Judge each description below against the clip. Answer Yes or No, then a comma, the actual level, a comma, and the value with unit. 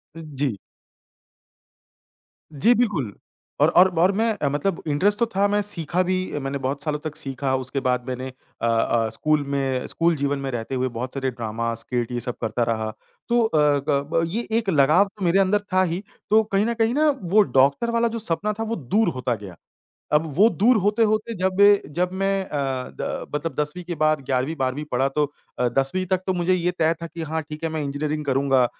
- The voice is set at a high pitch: No, medium, 155 Hz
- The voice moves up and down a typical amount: No, wide, 6.4 semitones